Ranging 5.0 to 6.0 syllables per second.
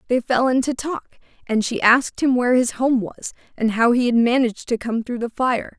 Yes: 5.5 syllables/s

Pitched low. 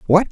No: medium, 180 Hz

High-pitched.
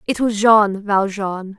Yes: high, 205 Hz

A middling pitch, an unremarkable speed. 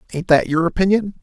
Yes: medium, 180 Hz; average, 195 wpm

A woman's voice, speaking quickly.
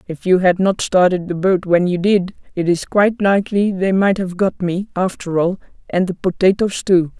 Yes: female; fast, 210 wpm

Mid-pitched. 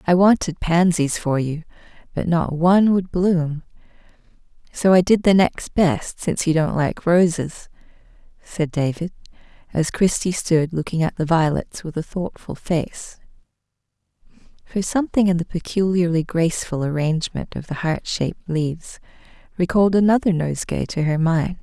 Yes: medium, 170 Hz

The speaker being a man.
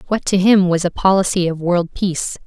No: female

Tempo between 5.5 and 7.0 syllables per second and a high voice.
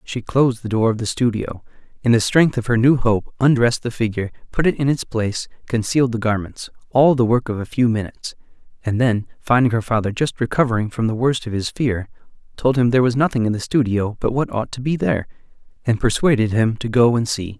No: 6.0 syllables/s; low, 120 Hz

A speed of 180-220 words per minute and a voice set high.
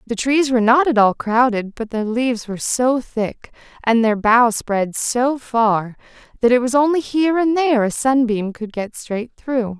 Yes: average, 195 wpm; high, 240 Hz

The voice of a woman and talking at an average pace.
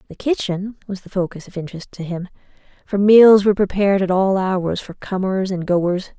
Yes: female; average, 195 wpm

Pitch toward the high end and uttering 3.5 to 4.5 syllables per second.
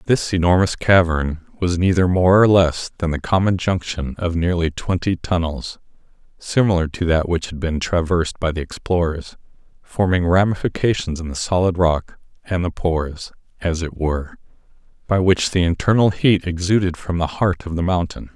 No: very low, 85 Hz; 4.3 syllables/s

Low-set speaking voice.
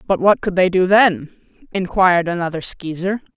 No: medium, 185 Hz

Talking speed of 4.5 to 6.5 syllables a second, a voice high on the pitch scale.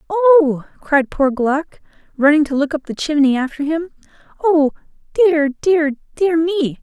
No: 4.0 syllables/s; very high, 300 Hz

